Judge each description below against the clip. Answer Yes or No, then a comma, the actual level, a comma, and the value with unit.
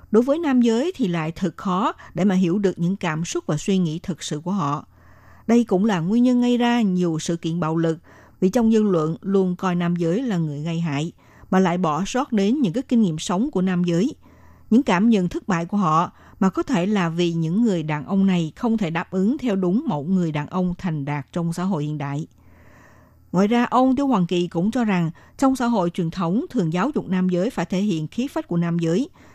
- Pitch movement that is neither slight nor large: Yes, average, 4.6 semitones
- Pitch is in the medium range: Yes, medium, 180 Hz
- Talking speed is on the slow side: No, average, 245 wpm